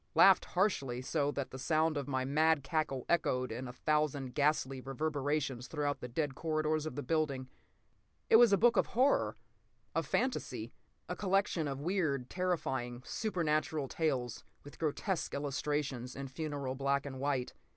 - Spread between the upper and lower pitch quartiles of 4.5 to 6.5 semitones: No, average, 3.2 semitones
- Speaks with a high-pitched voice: No, medium, 145 Hz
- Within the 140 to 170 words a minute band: Yes, average, 155 wpm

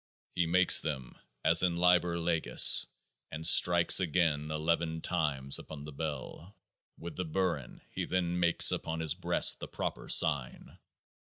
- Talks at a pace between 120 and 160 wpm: Yes, average, 145 wpm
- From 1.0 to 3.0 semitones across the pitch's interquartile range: Yes, narrow, 2.4 semitones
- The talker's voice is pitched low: Yes, very low, 80 Hz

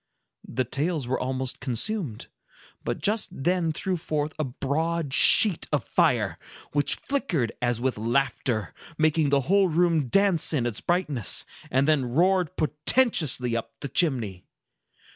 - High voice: No, medium, 150 Hz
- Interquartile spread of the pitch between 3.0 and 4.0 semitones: No, average, 5.2 semitones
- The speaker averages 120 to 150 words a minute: Yes, average, 140 wpm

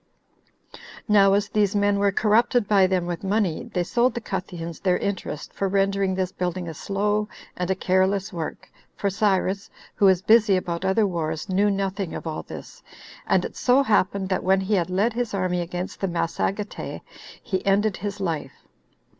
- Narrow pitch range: Yes, narrow, 2.0 semitones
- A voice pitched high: Yes, high, 195 Hz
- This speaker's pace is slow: No, average, 180 wpm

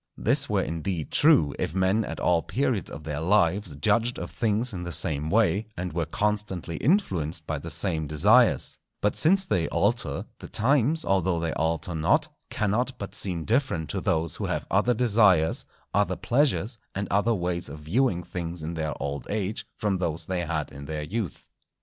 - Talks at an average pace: Yes, average, 180 wpm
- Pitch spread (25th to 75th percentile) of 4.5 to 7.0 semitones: Yes, average, 5.1 semitones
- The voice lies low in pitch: Yes, very low, 90 Hz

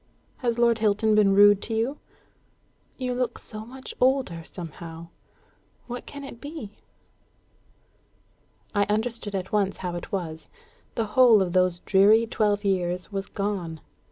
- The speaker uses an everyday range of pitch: Yes, average, 3.9 semitones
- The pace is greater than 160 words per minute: No, average, 140 wpm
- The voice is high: Yes, high, 205 Hz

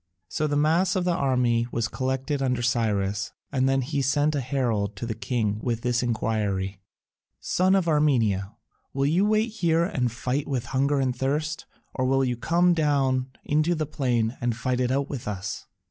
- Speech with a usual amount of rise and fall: Yes, average, 4.1 semitones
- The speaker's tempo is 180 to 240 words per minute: Yes, average, 185 wpm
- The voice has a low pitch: Yes, low, 130 Hz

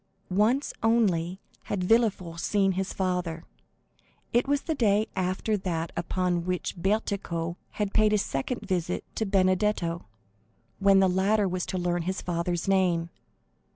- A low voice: No, medium, 185 Hz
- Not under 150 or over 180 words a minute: No, average, 140 wpm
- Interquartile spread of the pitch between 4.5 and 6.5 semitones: No, average, 3.0 semitones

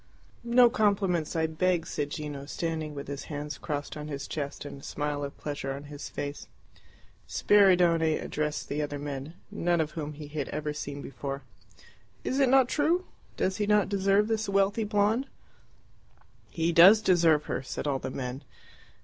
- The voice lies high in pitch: No, medium, 155 Hz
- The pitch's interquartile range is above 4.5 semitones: Yes, average, 5.3 semitones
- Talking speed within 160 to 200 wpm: Yes, average, 170 wpm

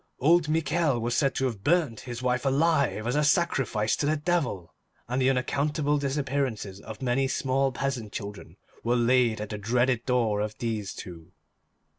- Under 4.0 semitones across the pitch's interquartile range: No, average, 4.3 semitones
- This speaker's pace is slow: No, average, 170 wpm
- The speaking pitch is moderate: No, low, 125 Hz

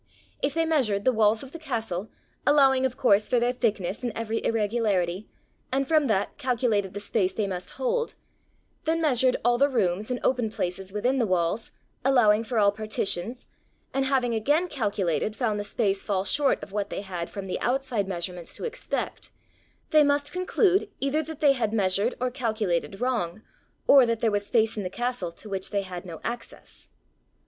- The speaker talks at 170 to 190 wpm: Yes, average, 185 wpm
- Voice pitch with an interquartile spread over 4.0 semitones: Yes, average, 4.8 semitones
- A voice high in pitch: Yes, high, 225 Hz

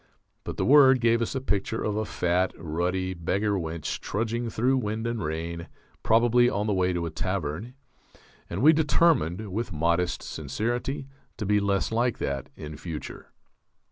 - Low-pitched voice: Yes, low, 105 Hz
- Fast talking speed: No, average, 165 wpm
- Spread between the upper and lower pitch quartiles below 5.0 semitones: No, wide, 5.4 semitones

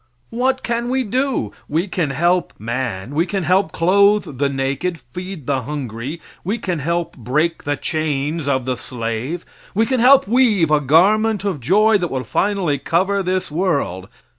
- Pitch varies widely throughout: Yes, wide, 6.5 semitones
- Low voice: No, medium, 170 Hz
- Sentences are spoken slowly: No, average, 165 wpm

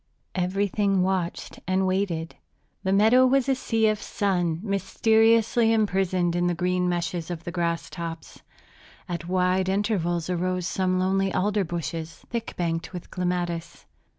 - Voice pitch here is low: No, medium, 185 Hz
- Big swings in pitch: No, narrow, 2.5 semitones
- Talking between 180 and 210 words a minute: No, average, 140 wpm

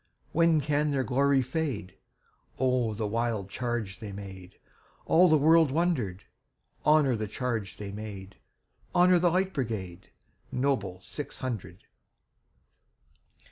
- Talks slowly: Yes, slow, 100 wpm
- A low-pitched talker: Yes, low, 125 Hz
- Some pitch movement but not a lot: No, wide, 6.8 semitones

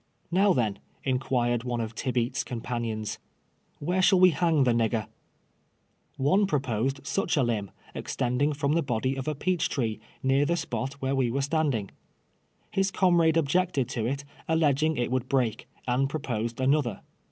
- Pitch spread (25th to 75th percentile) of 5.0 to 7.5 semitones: No, average, 4.5 semitones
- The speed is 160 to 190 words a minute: Yes, average, 170 wpm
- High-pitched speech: No, low, 135 Hz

